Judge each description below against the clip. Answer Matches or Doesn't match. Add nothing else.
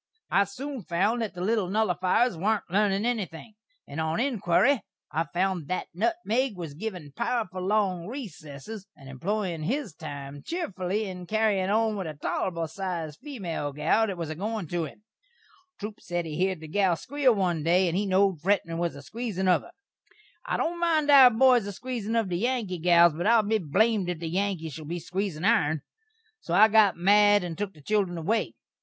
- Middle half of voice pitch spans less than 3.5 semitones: Doesn't match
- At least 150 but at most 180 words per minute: Doesn't match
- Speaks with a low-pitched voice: Doesn't match